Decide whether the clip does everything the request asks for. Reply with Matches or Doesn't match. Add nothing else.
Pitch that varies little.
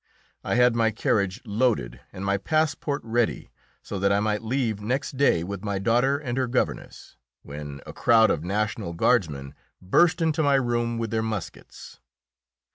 Doesn't match